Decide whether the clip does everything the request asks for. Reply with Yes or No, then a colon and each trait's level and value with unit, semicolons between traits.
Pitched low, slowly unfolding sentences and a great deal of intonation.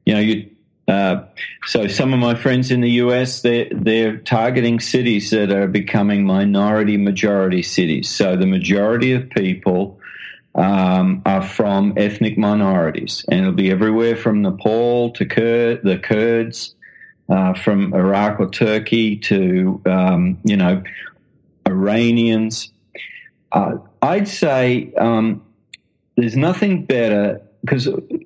No: low, 110 Hz; slow, 125 wpm; average, 3.2 semitones